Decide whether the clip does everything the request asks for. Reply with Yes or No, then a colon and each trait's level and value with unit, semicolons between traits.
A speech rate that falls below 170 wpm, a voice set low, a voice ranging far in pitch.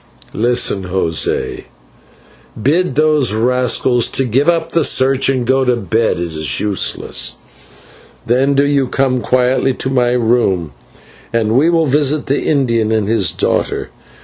No: average, 145 wpm; low, 125 Hz; average, 3.6 semitones